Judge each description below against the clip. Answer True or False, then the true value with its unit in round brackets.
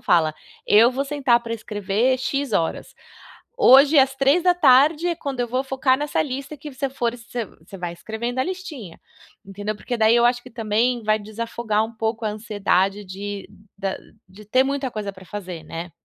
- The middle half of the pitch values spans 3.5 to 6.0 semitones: True (4.5 semitones)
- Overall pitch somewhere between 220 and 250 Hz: True (235 Hz)